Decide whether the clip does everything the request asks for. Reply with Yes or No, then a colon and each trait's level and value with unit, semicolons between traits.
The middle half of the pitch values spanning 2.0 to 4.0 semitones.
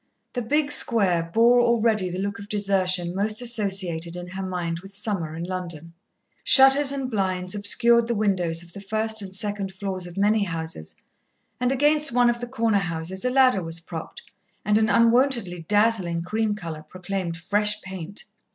No: average, 4.4 semitones